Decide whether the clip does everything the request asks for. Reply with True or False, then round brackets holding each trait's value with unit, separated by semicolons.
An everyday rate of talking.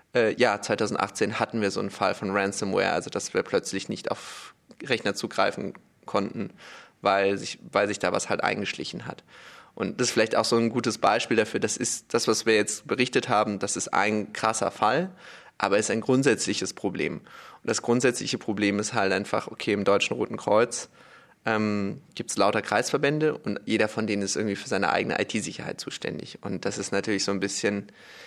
False (195 wpm)